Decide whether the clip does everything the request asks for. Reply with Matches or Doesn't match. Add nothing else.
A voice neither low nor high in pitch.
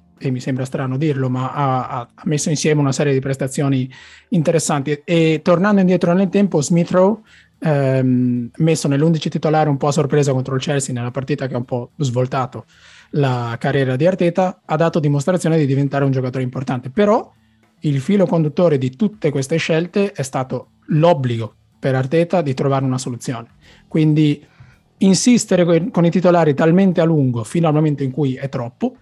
Matches